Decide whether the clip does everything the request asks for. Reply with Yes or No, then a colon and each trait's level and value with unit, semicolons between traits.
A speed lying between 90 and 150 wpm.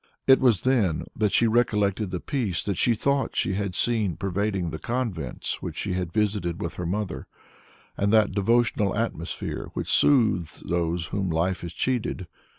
No: average, 165 wpm